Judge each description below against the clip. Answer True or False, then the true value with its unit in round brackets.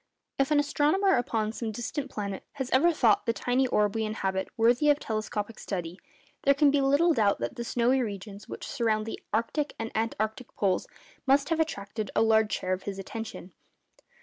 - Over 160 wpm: True (190 wpm)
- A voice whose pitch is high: True (225 Hz)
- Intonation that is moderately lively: True (4.6 semitones)